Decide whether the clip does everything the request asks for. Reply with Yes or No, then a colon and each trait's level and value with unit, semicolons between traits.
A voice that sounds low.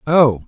Yes: low, 130 Hz